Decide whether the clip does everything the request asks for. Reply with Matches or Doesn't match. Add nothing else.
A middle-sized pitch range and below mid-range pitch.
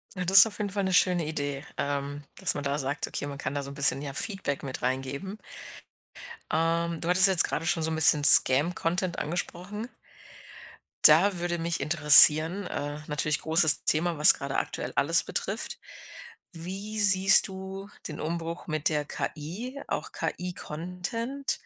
Doesn't match